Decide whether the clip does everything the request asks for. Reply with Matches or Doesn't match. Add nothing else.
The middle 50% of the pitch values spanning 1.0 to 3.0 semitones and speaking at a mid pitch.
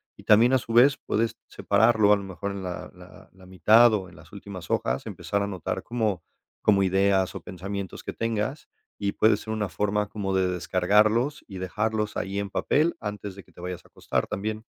Doesn't match